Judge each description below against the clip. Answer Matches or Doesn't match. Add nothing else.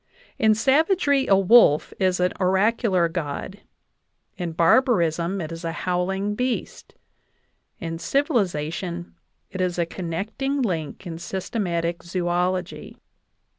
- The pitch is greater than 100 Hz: Matches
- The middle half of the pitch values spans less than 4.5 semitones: Matches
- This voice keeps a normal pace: Doesn't match